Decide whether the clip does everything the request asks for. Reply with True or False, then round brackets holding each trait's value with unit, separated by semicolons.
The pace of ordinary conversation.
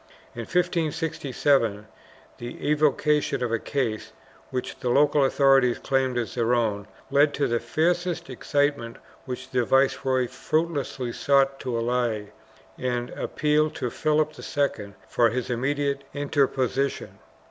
False (125 wpm)